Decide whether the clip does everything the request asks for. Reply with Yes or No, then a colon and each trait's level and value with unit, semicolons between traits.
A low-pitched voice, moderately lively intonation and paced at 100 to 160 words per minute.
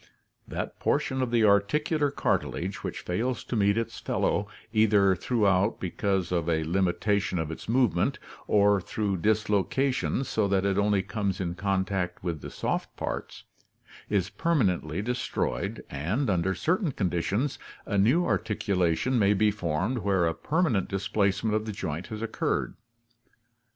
Yes: low, 100 Hz; average, 3.3 semitones; average, 145 wpm